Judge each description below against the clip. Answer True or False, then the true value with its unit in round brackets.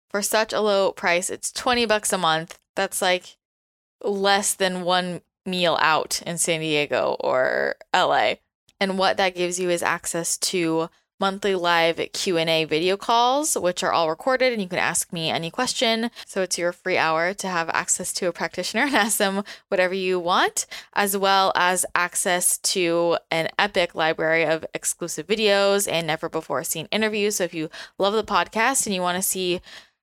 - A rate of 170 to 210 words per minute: True (185 wpm)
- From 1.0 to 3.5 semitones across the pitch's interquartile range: True (3.2 semitones)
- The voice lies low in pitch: False (185 Hz)